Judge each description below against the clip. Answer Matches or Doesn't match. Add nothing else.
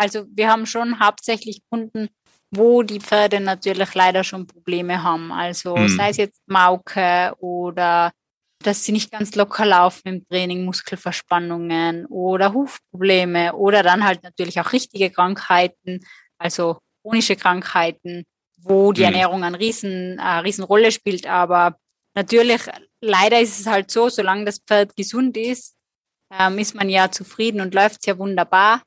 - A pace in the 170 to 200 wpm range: Doesn't match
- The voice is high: Matches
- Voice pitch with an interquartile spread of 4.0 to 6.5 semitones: Doesn't match